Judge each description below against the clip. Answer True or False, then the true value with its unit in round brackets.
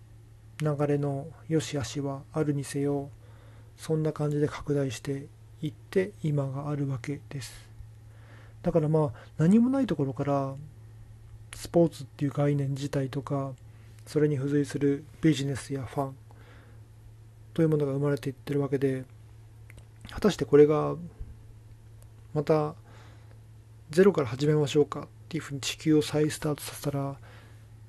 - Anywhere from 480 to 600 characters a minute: False (285 characters per minute)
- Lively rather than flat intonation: False (5.0 semitones)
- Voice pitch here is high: False (140 Hz)